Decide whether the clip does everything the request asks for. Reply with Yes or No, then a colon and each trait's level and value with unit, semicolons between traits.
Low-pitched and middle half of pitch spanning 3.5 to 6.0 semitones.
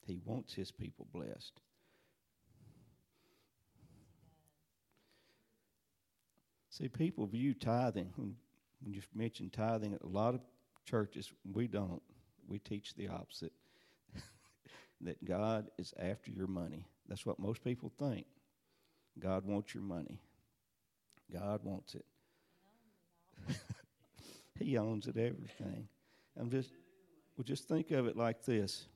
Yes: low, 110 Hz; average, 4.1 semitones